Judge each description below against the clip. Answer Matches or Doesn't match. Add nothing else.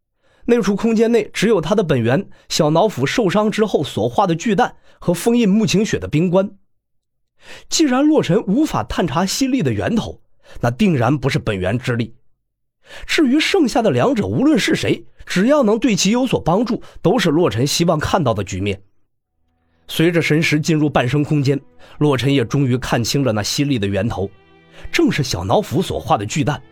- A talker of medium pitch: Matches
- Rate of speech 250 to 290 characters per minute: Matches